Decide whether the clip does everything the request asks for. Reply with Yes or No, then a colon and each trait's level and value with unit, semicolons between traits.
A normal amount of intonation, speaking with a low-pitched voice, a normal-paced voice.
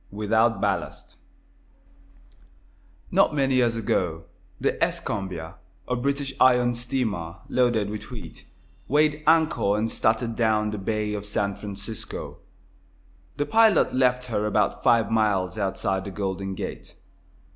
No: average, 3.9 semitones; low, 110 Hz; slow, 125 wpm